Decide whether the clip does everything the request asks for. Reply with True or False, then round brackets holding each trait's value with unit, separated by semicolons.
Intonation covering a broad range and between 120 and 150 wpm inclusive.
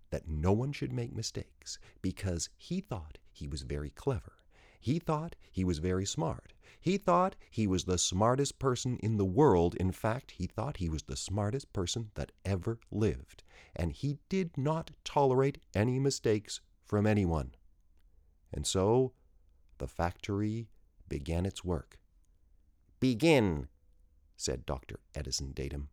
True (8.1 semitones; 145 wpm)